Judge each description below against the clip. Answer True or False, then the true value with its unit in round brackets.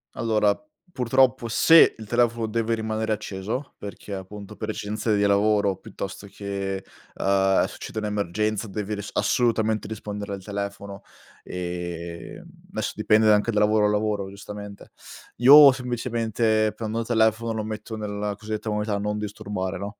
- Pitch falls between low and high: False (105 Hz)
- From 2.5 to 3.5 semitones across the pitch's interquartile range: False (1.8 semitones)